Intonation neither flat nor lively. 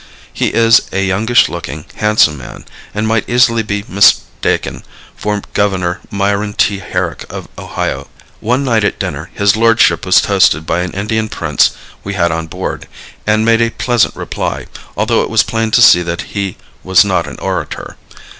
Yes: average, 3.4 semitones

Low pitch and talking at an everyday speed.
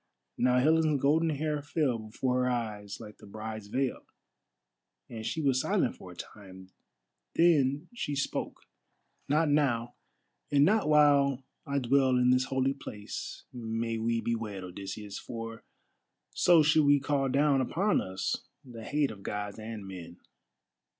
Yes: low, 125 Hz; average, 150 wpm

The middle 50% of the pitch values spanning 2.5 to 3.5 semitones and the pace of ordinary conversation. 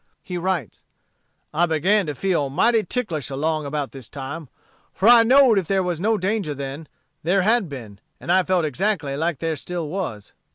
No: average, 5.1 semitones; average, 180 wpm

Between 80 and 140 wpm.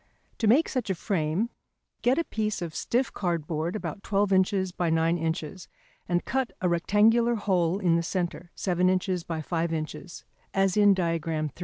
No: average, 175 wpm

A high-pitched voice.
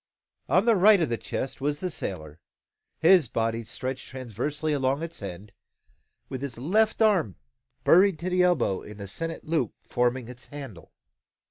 No: low, 135 Hz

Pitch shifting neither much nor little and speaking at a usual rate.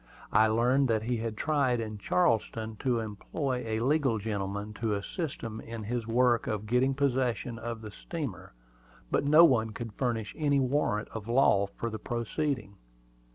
Yes: average, 3.2 semitones; average, 165 wpm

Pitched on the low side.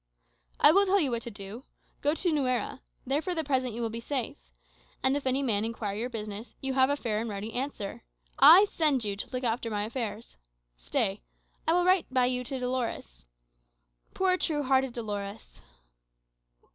No: very high, 250 Hz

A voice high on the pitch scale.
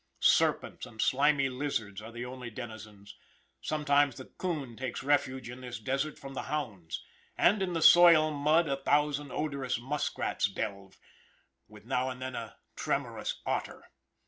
No: low, 130 Hz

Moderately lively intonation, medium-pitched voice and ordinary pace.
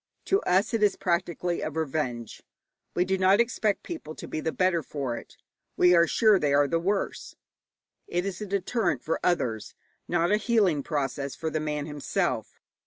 Yes: average, 4.6 semitones; medium, 175 Hz; average, 180 wpm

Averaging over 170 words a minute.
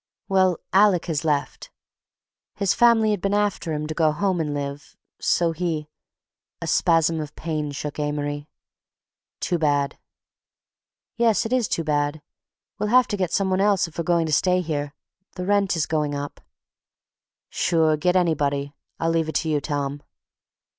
No: average, 160 wpm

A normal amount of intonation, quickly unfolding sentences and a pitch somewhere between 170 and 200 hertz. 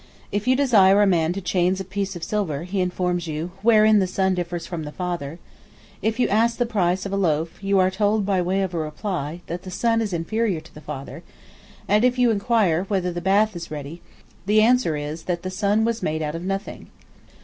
Yes: average, 3.6 semitones; fast, 220 wpm; high, 190 Hz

